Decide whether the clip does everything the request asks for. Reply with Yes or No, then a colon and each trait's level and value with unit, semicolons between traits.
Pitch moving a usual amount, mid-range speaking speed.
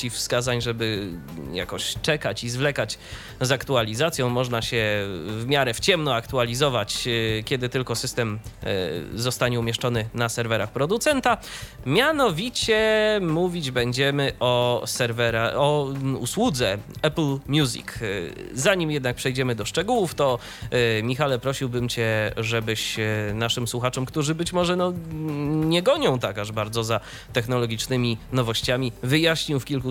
Yes: average, 4.1 semitones; average, 120 wpm